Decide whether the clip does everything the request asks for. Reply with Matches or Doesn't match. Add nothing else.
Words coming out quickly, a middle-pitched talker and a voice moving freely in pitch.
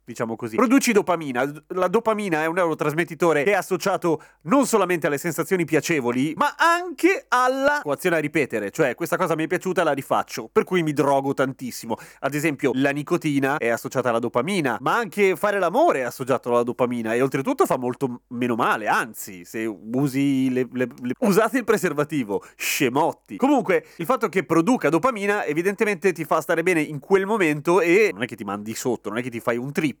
Matches